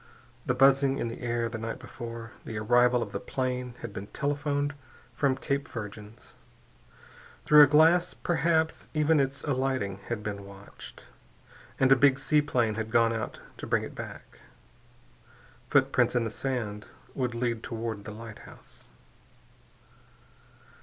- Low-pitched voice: Yes, low, 125 Hz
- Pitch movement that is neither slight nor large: Yes, average, 3.6 semitones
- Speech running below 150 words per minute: Yes, average, 140 wpm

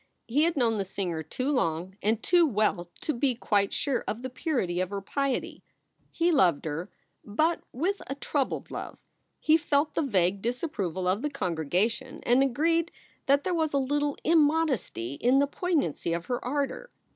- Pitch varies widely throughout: Yes, wide, 7.3 semitones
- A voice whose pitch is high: Yes, very high, 255 Hz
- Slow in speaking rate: No, average, 180 wpm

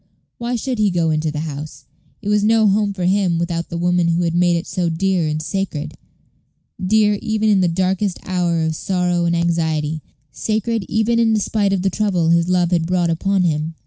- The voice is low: No, medium, 180 Hz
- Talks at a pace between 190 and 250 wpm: Yes, fast, 205 wpm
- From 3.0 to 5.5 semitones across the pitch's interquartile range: Yes, average, 3.4 semitones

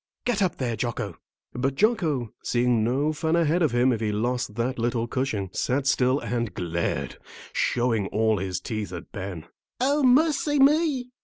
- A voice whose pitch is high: No, low, 125 Hz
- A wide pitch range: Yes, wide, 7.3 semitones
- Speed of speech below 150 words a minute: No, average, 165 wpm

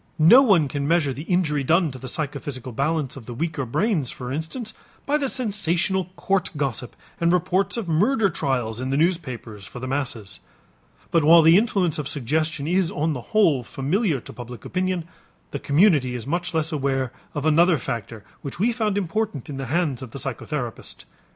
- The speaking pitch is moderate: Yes, medium, 155 Hz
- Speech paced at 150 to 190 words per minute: Yes, average, 185 wpm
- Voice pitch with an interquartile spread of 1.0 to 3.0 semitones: No, average, 5.3 semitones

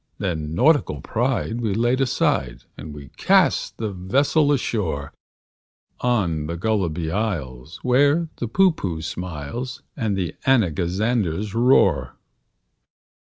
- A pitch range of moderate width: No, wide, 7.3 semitones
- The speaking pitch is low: Yes, low, 100 Hz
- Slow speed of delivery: Yes, slow, 110 wpm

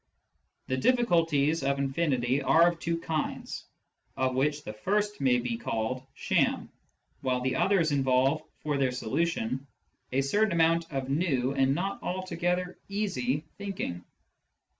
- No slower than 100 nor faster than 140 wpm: Yes, slow, 135 wpm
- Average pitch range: Yes, average, 4.6 semitones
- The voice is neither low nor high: Yes, medium, 145 Hz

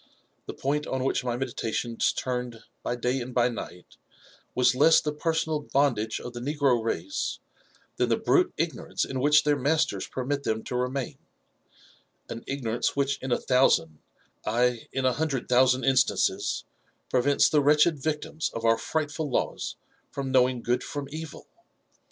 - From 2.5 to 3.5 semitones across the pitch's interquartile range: Yes, average, 3.0 semitones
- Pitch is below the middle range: Yes, low, 130 Hz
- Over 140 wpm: Yes, average, 165 wpm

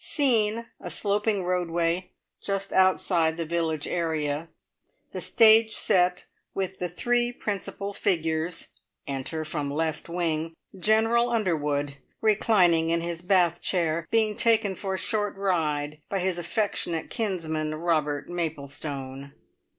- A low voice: No, medium, 175 Hz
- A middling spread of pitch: Yes, average, 4.1 semitones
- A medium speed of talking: No, slow, 120 wpm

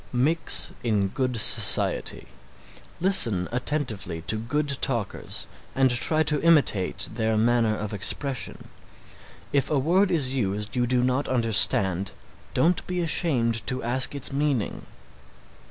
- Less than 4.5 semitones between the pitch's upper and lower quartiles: No, average, 4.9 semitones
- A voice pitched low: Yes, low, 125 Hz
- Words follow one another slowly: Yes, slow, 125 wpm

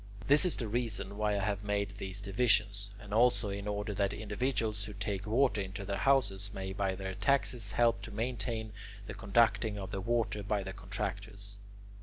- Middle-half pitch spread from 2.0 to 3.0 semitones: Yes, narrow, 2.4 semitones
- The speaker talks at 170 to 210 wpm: Yes, average, 185 wpm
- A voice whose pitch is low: Yes, low, 105 Hz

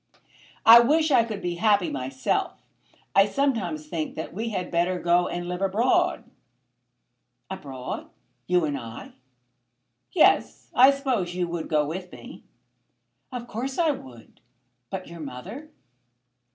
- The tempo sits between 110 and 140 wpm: Yes, slow, 135 wpm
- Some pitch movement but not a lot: No, wide, 6.2 semitones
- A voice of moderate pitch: Yes, medium, 180 Hz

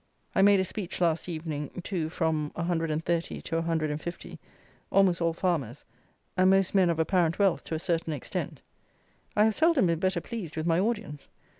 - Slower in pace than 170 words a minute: No, average, 175 wpm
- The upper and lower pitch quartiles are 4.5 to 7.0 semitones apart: No, average, 2.8 semitones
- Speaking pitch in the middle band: Yes, medium, 170 Hz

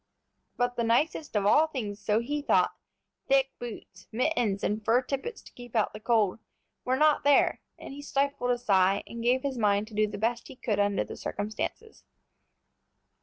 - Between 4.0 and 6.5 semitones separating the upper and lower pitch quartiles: Yes, average, 4.5 semitones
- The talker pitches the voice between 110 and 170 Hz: No, high, 235 Hz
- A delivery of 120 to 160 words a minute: No, average, 185 wpm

